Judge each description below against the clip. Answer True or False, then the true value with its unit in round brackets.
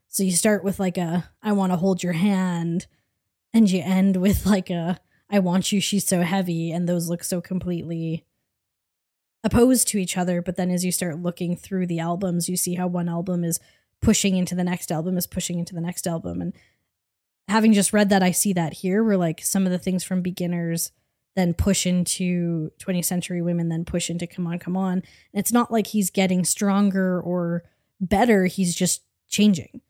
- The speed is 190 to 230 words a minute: True (205 wpm)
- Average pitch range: False (1.9 semitones)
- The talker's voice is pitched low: False (180 Hz)